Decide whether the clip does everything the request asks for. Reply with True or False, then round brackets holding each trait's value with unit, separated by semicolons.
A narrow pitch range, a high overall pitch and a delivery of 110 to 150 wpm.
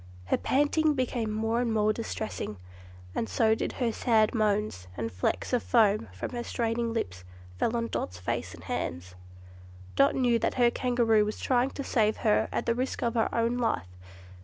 False (2.3 semitones; 230 Hz; 185 wpm)